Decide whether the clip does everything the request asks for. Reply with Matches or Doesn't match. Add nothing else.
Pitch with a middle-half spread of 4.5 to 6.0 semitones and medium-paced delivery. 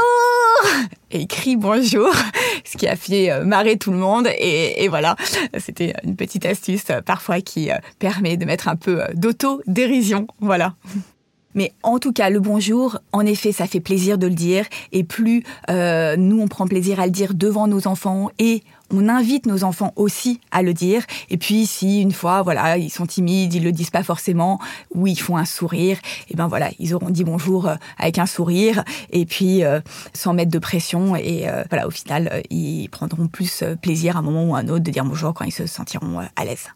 Doesn't match